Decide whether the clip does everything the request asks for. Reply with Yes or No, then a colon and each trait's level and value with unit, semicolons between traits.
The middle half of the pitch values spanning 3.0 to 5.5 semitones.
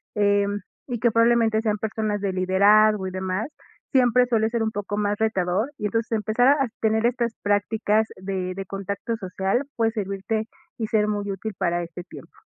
No: narrow, 2.4 semitones